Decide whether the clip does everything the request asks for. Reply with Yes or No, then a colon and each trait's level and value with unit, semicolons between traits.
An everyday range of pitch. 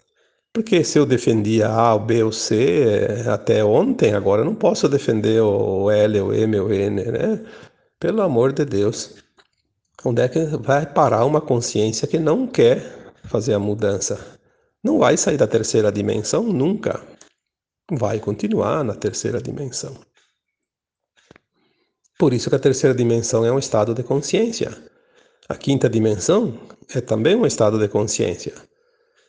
No: wide, 6.9 semitones